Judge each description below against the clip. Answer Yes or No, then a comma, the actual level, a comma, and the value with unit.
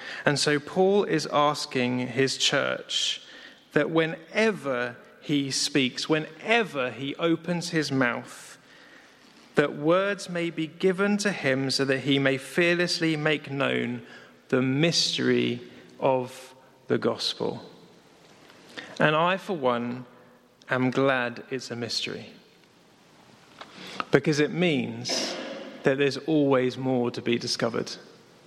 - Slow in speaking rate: Yes, slow, 115 wpm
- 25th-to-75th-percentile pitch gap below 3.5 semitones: No, average, 4.4 semitones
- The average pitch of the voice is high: No, medium, 140 Hz